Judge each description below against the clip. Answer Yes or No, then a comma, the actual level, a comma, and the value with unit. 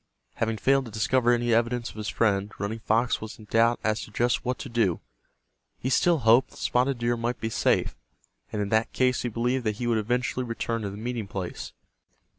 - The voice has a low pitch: Yes, low, 115 Hz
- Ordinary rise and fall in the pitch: No, narrow, 2.1 semitones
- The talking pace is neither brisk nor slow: No, fast, 215 wpm